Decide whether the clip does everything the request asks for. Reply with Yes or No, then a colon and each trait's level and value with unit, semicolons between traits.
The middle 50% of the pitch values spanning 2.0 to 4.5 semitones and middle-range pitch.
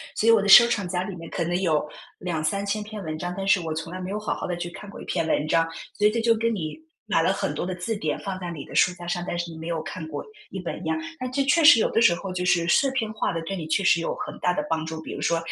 Yes: average, 4.0 semitones; medium, 180 Hz